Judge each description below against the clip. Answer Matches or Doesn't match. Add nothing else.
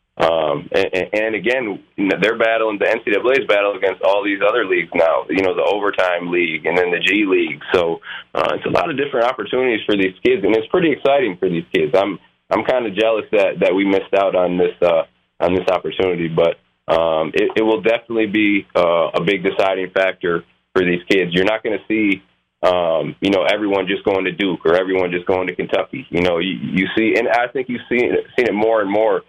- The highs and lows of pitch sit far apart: Matches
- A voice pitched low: Matches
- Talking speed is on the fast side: Matches